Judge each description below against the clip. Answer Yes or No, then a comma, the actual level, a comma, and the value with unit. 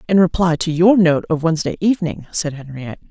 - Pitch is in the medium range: Yes, medium, 165 Hz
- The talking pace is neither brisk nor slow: Yes, average, 195 wpm